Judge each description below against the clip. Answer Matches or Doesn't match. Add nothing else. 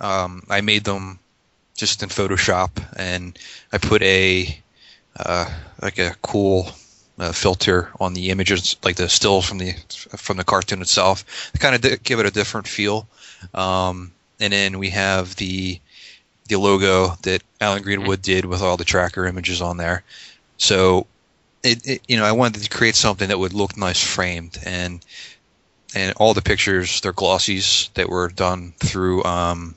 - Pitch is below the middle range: Matches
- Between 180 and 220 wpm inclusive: Doesn't match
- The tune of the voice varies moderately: Doesn't match